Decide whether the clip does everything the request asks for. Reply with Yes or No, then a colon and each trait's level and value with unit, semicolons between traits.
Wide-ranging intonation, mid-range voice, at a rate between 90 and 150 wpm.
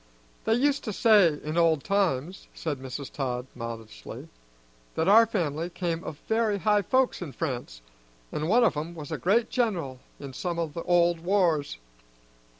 No: wide, 5.9 semitones; medium, 170 Hz; average, 165 wpm